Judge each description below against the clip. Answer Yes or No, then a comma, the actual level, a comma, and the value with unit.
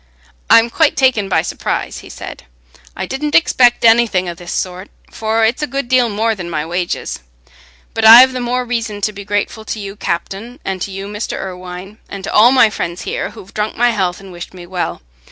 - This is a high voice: Yes, high, 210 Hz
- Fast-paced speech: Yes, fast, 210 wpm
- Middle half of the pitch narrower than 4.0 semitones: No, average, 4.4 semitones